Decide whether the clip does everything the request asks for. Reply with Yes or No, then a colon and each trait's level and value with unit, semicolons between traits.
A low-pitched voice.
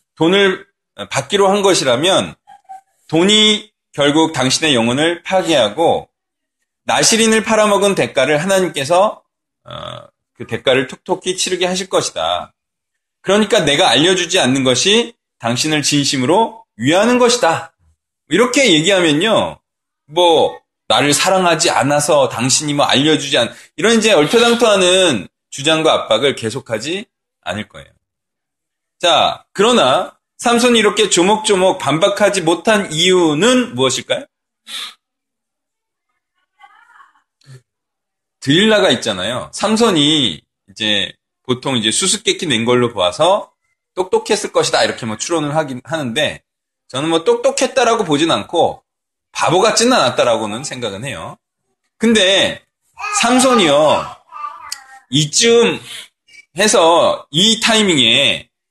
No: medium, 185 Hz